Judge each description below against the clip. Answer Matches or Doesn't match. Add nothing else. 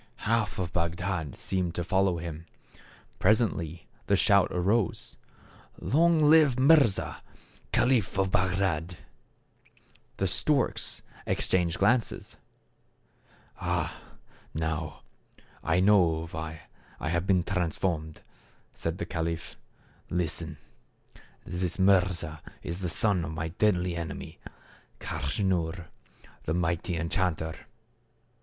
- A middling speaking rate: Doesn't match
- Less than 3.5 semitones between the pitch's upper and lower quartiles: Matches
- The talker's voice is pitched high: Doesn't match